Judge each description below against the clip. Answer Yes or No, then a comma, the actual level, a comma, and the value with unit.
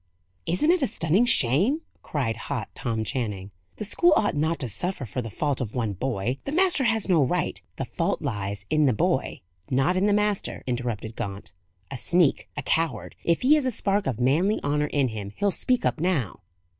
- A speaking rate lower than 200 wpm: No, fast, 205 wpm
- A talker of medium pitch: Yes, medium, 145 Hz